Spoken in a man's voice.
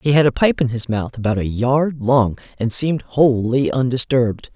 No: female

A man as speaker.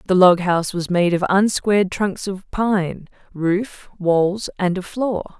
No: female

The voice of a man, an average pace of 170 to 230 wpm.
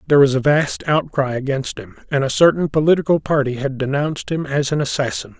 Yes: male; average, 200 wpm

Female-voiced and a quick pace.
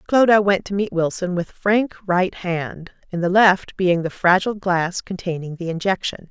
No: female; average, 180 wpm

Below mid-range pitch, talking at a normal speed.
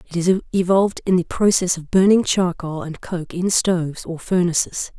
No: medium, 175 Hz; average, 180 wpm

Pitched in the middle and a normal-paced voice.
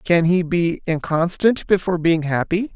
Yes: medium, 175 Hz; average, 155 wpm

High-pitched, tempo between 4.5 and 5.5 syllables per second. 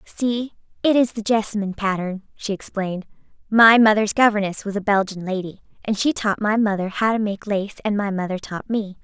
No: high, 205 Hz; 5.7 syllables/s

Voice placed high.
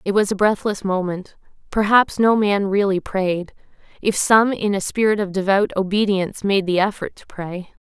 Yes: high, 200 Hz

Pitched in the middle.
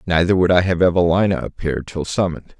No: very low, 85 Hz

